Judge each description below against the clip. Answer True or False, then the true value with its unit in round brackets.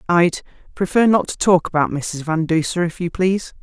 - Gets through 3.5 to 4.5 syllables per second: False (5.3 syllables/s)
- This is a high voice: False (170 Hz)